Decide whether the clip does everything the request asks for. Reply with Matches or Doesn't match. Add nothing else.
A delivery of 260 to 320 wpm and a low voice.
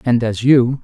Doesn't match